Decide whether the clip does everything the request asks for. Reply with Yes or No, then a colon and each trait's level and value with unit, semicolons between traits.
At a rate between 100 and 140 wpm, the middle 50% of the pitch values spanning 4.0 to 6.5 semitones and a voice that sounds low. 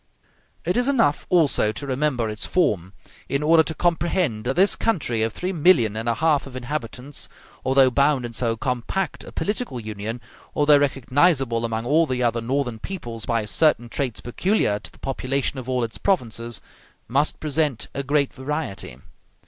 No: average, 170 wpm; average, 4.7 semitones; low, 130 Hz